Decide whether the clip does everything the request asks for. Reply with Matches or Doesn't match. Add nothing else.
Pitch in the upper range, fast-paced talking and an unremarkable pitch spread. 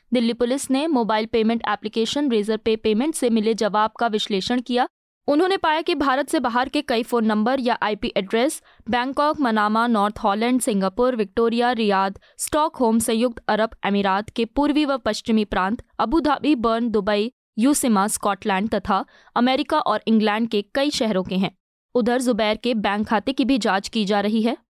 Doesn't match